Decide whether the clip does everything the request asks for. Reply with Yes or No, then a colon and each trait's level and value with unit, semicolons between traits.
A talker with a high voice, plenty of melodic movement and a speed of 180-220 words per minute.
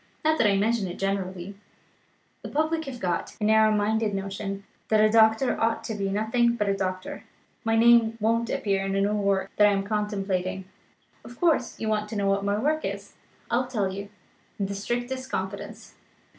No: high, 210 Hz; narrow, 2.6 semitones; average, 200 wpm